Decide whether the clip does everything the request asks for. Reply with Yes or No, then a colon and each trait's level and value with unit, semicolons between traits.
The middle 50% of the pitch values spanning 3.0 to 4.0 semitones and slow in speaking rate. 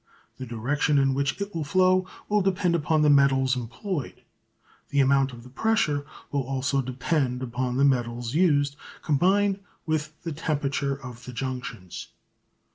No: average, 3.6 semitones; average, 150 wpm